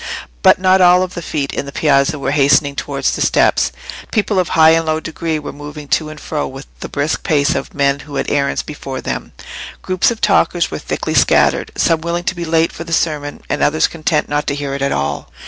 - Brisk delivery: Yes, fast, 225 wpm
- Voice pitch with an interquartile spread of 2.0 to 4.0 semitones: Yes, average, 2.9 semitones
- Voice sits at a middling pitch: Yes, medium, 150 Hz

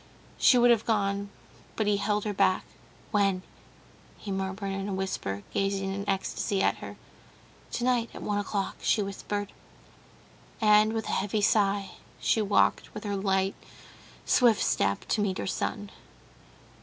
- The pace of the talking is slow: No, average, 150 wpm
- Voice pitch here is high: Yes, high, 200 Hz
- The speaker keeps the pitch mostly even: Yes, narrow, 1.5 semitones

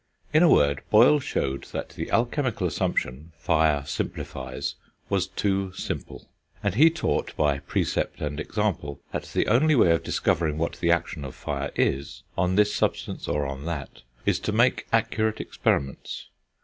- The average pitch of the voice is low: Yes, very low, 85 Hz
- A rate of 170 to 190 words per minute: No, average, 160 wpm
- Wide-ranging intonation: Yes, wide, 7.2 semitones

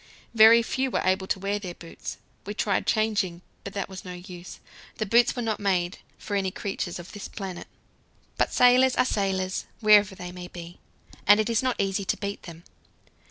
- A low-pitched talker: No, high, 200 Hz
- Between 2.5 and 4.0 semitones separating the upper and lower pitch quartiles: Yes, average, 2.9 semitones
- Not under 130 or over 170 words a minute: No, average, 190 wpm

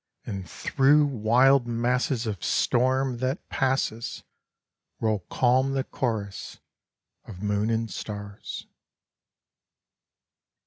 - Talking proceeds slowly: Yes, slow, 90 wpm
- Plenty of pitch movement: No, average, 3.6 semitones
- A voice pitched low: Yes, low, 120 Hz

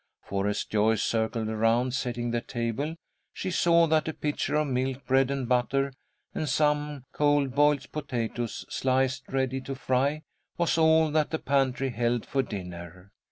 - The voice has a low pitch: Yes, low, 130 Hz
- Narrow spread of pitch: No, average, 3.7 semitones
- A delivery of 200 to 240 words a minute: No, average, 160 wpm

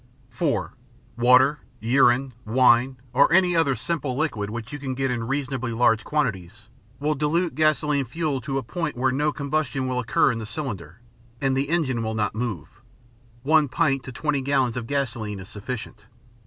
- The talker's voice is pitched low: Yes, low, 130 Hz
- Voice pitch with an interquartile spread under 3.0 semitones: No, average, 4.0 semitones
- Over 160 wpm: Yes, average, 170 wpm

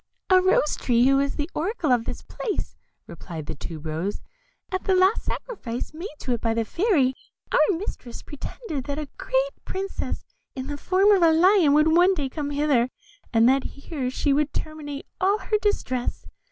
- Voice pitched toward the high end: Yes, very high, 295 Hz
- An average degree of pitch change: No, wide, 6.4 semitones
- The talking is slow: No, average, 185 wpm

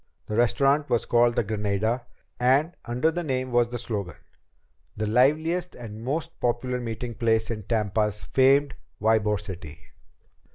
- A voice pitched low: Yes, low, 120 Hz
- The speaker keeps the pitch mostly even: No, average, 3.5 semitones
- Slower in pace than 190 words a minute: Yes, average, 140 wpm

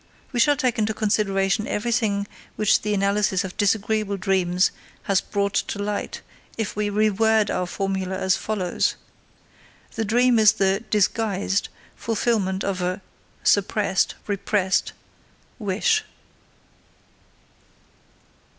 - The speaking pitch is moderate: No, high, 205 Hz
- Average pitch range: No, narrow, 2.1 semitones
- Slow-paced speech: Yes, slow, 110 wpm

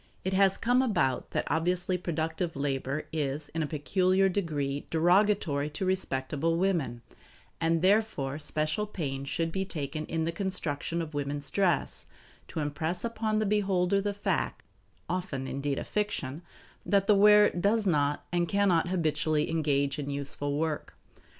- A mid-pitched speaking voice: Yes, medium, 165 Hz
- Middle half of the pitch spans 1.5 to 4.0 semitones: No, average, 4.9 semitones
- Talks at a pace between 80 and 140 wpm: No, average, 150 wpm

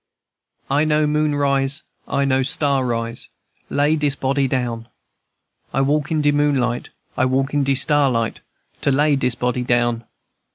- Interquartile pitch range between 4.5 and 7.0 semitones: No, average, 2.7 semitones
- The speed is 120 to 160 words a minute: Yes, average, 155 wpm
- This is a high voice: No, low, 135 Hz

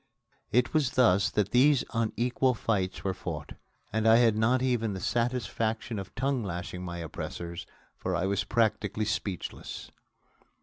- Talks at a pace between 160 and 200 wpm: No, average, 145 wpm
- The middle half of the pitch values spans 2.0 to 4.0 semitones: No, average, 4.4 semitones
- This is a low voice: Yes, low, 110 Hz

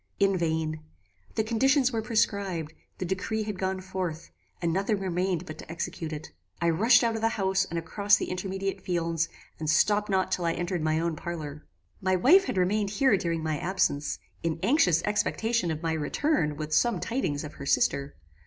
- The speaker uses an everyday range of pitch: Yes, average, 4.3 semitones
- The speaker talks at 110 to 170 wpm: No, average, 190 wpm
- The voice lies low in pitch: No, medium, 185 Hz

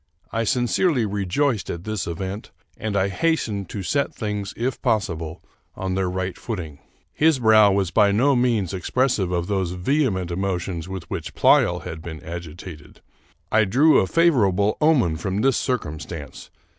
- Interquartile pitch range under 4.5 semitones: No, average, 5.1 semitones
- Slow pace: No, average, 155 wpm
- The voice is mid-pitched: No, low, 100 Hz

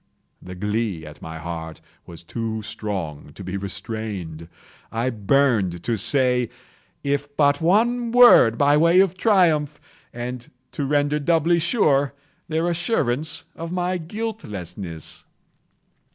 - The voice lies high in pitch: No, low, 130 Hz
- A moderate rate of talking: No, slow, 125 wpm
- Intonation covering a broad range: Yes, wide, 8.7 semitones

